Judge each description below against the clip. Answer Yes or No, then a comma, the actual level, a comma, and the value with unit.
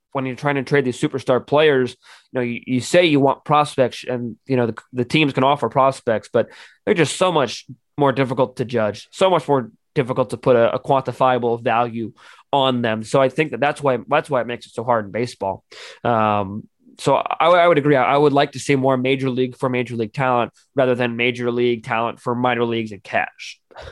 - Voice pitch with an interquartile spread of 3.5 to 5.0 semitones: No, average, 2.7 semitones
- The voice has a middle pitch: No, low, 130 Hz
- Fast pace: Yes, fast, 225 wpm